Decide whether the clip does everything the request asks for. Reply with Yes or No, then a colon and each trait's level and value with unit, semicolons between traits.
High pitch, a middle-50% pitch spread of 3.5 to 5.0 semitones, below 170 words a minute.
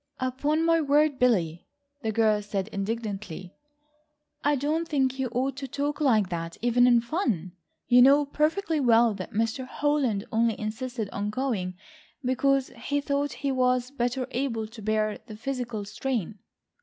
Yes: high, 245 Hz; average, 4.4 semitones; average, 155 wpm